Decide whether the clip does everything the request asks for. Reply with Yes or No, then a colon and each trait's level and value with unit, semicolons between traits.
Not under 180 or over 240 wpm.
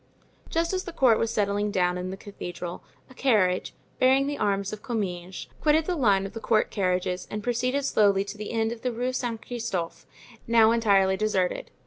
Yes: average, 190 wpm